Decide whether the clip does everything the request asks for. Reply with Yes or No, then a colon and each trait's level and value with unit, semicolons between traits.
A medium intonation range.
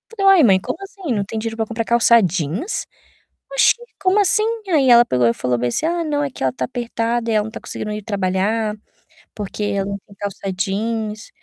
Yes: average, 3.7 semitones